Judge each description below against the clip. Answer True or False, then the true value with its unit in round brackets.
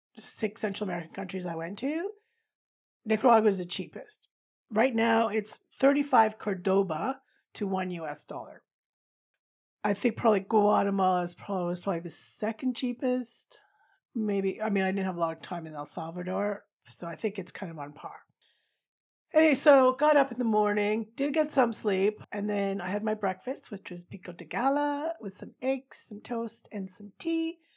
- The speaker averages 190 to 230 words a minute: False (180 wpm)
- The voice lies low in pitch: False (210 Hz)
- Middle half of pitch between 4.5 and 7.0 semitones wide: True (5.0 semitones)